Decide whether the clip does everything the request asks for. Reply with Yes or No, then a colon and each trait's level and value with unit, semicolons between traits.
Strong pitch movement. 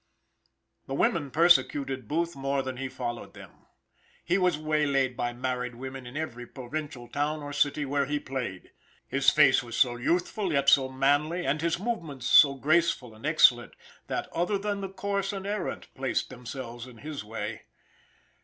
No: average, 4.6 semitones